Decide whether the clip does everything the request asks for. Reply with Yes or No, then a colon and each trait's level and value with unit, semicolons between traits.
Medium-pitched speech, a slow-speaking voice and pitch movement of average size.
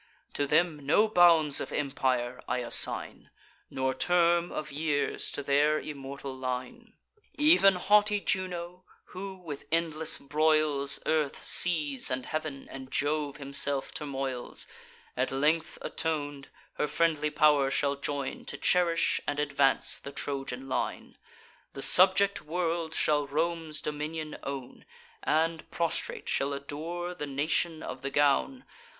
Yes: medium, 150 Hz; slow, 130 wpm; average, 3.2 semitones